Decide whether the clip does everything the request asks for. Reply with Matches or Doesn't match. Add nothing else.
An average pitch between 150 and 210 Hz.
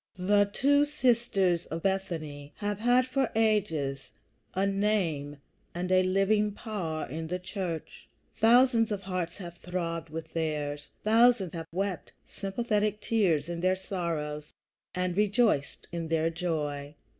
Matches